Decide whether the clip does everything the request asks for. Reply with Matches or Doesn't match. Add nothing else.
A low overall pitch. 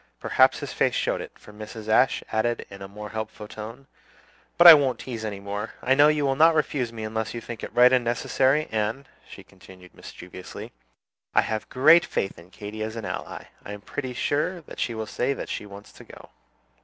Matches